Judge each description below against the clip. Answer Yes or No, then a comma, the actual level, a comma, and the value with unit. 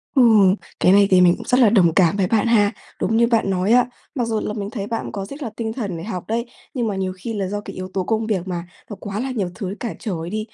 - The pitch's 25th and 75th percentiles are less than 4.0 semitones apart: Yes, average, 3.4 semitones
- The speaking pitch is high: Yes, high, 210 Hz